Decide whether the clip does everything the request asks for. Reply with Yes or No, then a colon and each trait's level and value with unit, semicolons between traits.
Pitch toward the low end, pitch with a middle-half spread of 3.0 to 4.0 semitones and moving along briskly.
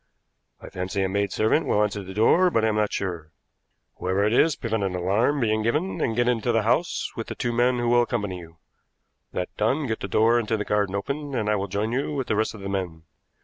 Yes: low, 110 Hz; average, 3.4 semitones; fast, 240 wpm